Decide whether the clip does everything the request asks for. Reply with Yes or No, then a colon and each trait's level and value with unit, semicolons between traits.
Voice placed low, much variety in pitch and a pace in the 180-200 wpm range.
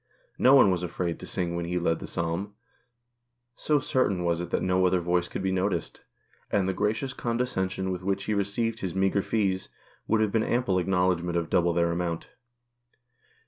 No: very low, 95 Hz; average, 2.8 semitones; average, 185 wpm